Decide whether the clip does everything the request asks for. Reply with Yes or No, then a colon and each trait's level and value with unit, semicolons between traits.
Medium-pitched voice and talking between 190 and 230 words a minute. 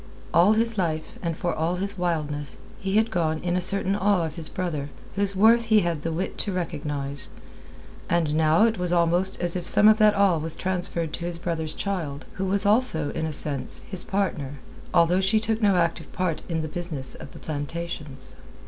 Yes: medium, 175 Hz; average, 200 wpm